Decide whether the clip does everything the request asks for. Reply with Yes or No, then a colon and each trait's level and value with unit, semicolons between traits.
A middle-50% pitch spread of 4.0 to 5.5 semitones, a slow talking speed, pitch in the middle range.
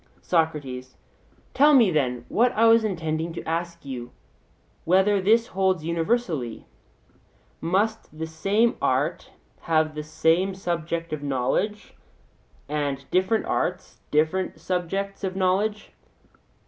Yes: average, 4.3 semitones; slow, 115 wpm; medium, 175 Hz